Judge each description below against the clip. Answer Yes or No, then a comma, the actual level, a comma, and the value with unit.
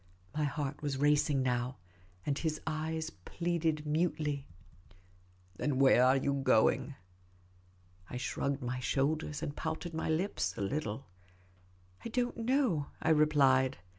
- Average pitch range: Yes, average, 4.3 semitones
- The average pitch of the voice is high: No, medium, 140 Hz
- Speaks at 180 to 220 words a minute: No, average, 140 wpm